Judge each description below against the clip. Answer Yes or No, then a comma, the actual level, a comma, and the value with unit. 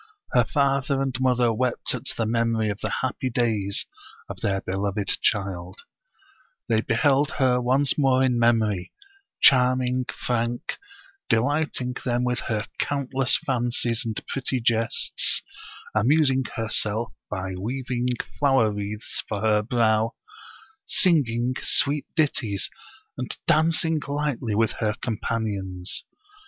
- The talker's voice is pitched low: Yes, low, 120 Hz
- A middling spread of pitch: Yes, average, 3.4 semitones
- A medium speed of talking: No, slow, 120 wpm